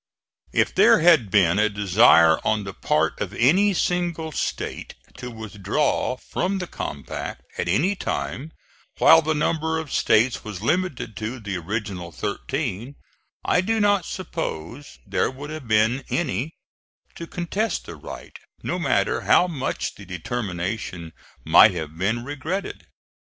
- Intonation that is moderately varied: No, wide, 8.2 semitones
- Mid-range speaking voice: No, low, 125 Hz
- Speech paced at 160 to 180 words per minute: No, average, 140 wpm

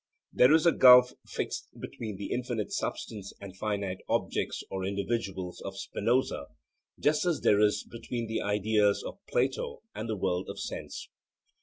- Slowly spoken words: No, average, 155 wpm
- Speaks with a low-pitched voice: Yes, low, 105 Hz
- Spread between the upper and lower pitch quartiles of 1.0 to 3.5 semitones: No, average, 4.0 semitones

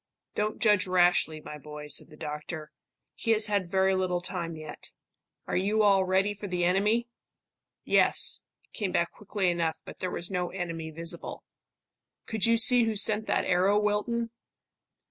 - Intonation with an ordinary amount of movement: Yes, average, 3.5 semitones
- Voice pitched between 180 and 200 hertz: Yes, medium, 185 Hz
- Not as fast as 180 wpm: Yes, average, 165 wpm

